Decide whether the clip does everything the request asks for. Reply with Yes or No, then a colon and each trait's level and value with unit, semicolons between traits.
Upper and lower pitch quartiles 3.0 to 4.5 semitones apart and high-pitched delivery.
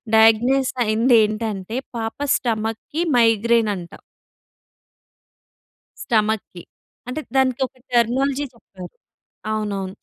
No: narrow, 2.5 semitones; high, 225 Hz